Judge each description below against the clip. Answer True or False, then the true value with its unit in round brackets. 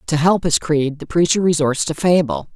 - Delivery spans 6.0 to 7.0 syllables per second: False (5.0 syllables/s)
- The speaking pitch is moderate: True (160 Hz)